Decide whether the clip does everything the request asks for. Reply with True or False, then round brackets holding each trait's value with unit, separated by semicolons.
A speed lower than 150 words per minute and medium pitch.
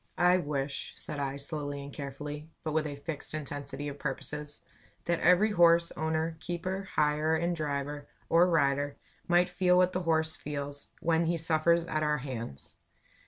False (165 wpm; 155 Hz)